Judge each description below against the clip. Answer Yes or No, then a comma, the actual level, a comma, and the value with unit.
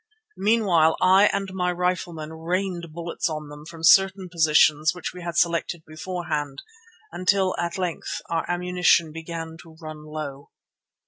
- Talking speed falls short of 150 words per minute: Yes, average, 140 wpm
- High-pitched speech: No, medium, 170 Hz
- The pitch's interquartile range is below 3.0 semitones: Yes, narrow, 2.4 semitones